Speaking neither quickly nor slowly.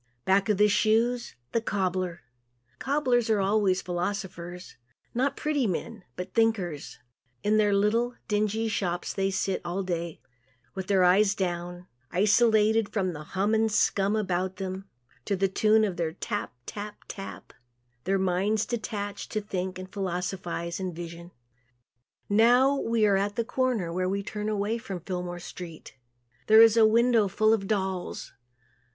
Yes: average, 155 wpm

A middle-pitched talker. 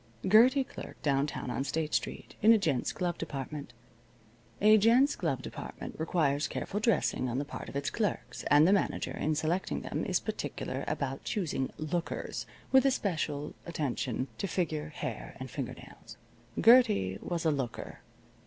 Yes: medium, 160 Hz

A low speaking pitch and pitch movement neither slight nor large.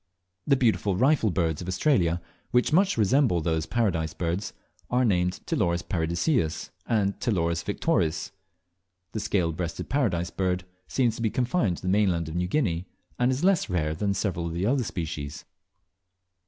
No: very low, 95 Hz; wide, 6.0 semitones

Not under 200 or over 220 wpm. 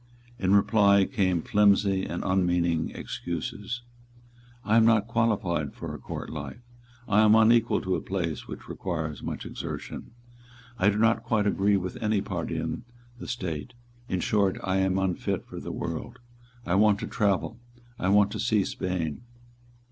No: average, 160 wpm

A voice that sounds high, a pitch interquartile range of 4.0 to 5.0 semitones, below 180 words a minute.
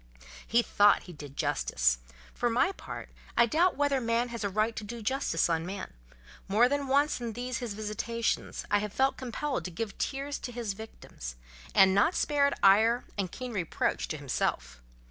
No: high, 230 Hz; average, 4.4 semitones; average, 185 wpm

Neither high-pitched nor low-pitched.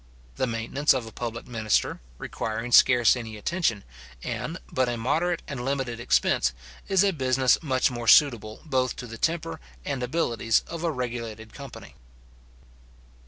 No: low, 125 Hz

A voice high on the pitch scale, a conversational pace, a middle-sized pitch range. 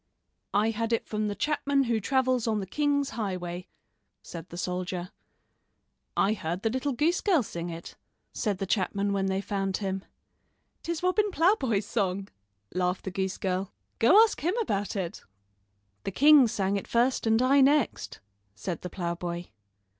No: high, 205 Hz; average, 160 wpm; wide, 6.0 semitones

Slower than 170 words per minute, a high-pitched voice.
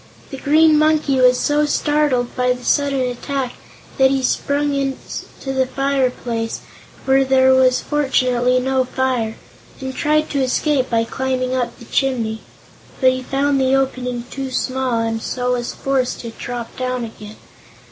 Yes: average, 155 wpm; very high, 260 Hz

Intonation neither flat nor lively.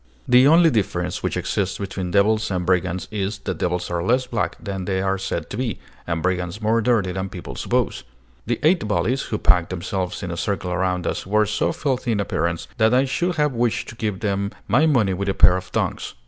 Yes: average, 4.0 semitones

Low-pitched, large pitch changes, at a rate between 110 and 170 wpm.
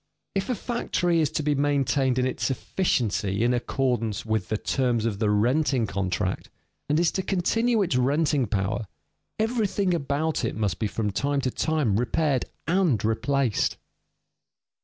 Yes: low, 130 Hz; wide, 6.2 semitones; average, 155 wpm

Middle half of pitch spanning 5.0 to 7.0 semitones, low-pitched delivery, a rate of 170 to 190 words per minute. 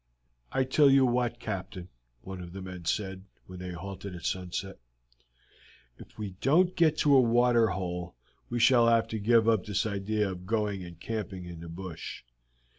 No: average, 4.3 semitones; low, 100 Hz; average, 180 wpm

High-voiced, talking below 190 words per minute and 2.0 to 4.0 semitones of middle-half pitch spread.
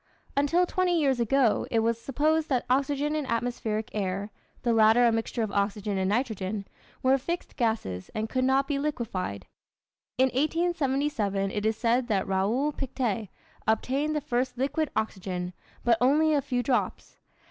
No: high, 245 Hz; average, 160 wpm; average, 4.7 semitones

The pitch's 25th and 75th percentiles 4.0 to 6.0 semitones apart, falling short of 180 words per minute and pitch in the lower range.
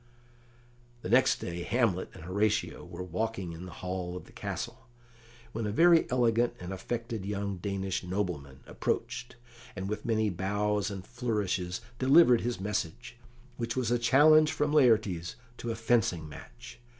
Yes: average, 4.5 semitones; average, 150 wpm; low, 105 Hz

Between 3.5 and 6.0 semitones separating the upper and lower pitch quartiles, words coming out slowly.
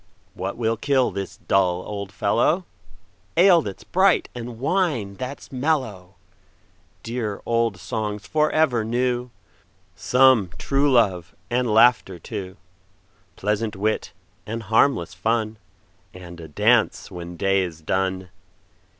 Yes: average, 4.9 semitones; slow, 110 wpm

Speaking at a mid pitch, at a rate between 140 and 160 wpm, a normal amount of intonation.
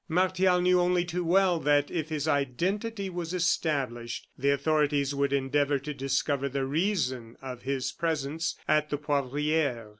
Yes: medium, 150 Hz; average, 150 wpm; average, 4.0 semitones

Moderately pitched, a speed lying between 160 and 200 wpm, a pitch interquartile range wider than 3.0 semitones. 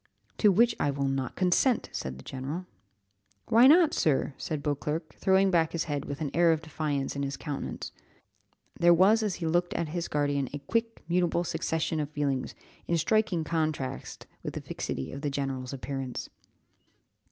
Yes: medium, 155 Hz; average, 175 wpm; average, 3.9 semitones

